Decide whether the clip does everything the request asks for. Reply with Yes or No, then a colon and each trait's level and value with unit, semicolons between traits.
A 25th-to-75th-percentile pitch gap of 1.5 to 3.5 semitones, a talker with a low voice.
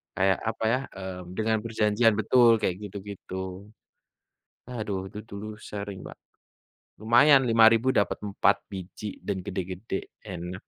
Yes: average, 2.9 semitones; low, 105 Hz